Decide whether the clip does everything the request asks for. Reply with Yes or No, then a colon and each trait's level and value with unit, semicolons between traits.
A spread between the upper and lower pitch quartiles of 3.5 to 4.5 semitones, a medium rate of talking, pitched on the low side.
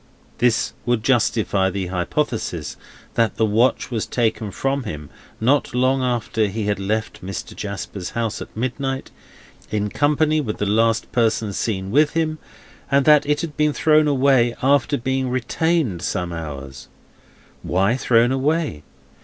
No: average, 5.1 semitones; average, 145 wpm; low, 120 Hz